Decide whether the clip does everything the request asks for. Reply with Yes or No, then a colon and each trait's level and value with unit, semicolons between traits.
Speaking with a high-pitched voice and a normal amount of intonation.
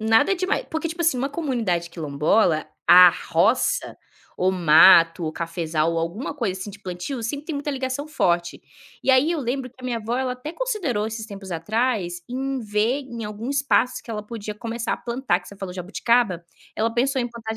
No: high, 225 Hz; wide, 6.4 semitones